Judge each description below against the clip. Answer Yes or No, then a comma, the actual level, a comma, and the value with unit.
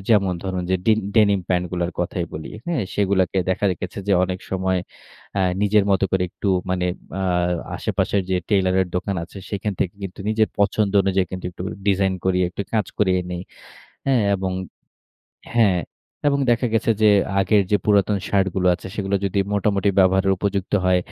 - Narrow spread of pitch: Yes, narrow, 1.8 semitones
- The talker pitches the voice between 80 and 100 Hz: Yes, very low, 95 Hz